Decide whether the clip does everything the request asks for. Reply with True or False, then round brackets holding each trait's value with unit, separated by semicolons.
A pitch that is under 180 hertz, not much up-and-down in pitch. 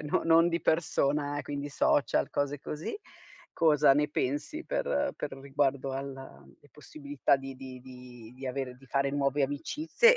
True (140 Hz; 1.9 semitones)